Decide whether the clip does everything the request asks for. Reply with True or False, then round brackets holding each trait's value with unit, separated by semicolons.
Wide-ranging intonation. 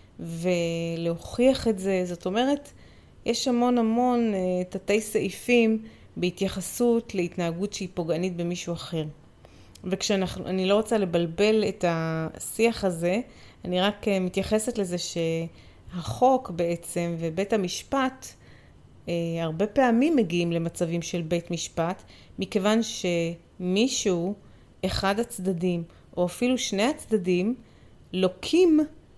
False (4.5 semitones)